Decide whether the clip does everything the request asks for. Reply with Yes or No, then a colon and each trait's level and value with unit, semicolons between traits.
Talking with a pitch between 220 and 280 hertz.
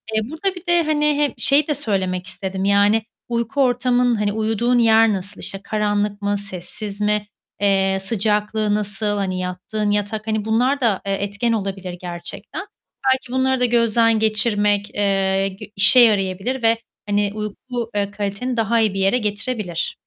No: high, 210 Hz